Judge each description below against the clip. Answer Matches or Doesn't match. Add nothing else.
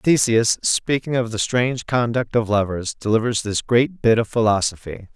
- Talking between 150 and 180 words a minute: Matches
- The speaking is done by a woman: Doesn't match